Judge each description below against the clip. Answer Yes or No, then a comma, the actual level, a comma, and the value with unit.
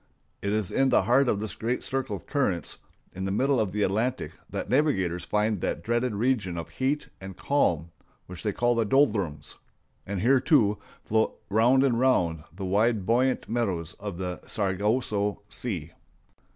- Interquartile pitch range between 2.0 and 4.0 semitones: No, average, 4.9 semitones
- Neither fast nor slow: Yes, average, 170 wpm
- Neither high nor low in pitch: No, low, 105 Hz